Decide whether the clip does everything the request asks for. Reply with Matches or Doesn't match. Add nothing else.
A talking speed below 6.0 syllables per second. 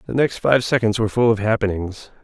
Doesn't match